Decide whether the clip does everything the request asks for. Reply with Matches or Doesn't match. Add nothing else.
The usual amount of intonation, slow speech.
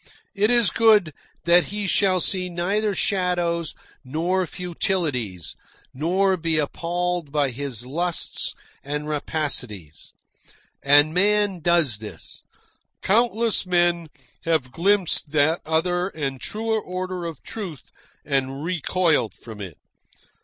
Matches